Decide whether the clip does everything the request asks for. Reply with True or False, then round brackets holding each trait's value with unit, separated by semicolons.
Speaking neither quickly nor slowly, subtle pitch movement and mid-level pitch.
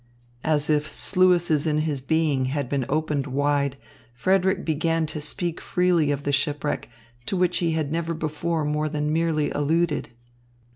True (155 wpm; 2.3 semitones; 155 Hz)